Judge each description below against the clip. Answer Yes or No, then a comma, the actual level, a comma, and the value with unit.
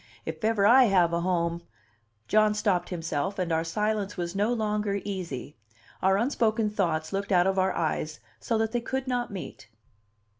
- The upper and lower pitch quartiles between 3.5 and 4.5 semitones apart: Yes, average, 4.1 semitones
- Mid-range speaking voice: No, high, 195 Hz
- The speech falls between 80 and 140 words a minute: No, average, 180 wpm